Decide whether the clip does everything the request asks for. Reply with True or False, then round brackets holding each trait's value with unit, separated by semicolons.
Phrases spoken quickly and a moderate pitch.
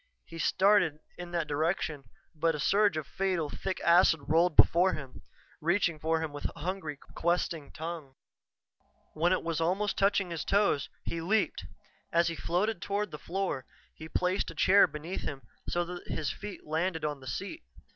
False (170 wpm; 170 Hz)